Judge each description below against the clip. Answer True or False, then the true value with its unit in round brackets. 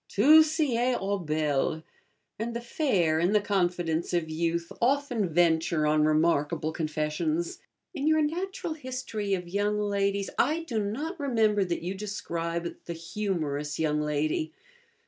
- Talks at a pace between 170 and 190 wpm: False (145 wpm)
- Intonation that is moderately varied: False (6.6 semitones)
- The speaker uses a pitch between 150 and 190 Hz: True (185 Hz)